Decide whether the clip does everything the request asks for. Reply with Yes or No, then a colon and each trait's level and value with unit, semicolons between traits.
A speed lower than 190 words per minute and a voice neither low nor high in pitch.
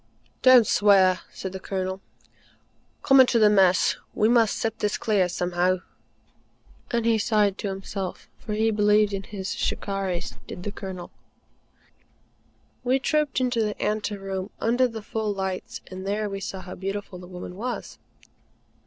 No: average, 155 wpm; high, 205 Hz